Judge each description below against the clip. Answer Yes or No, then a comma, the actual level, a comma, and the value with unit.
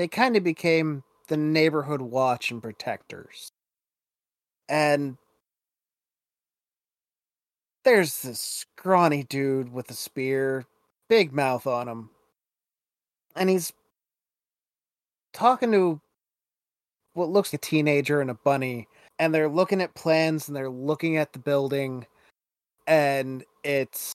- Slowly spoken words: Yes, slow, 115 wpm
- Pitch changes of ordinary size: Yes, average, 3.7 semitones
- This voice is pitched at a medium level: Yes, medium, 145 Hz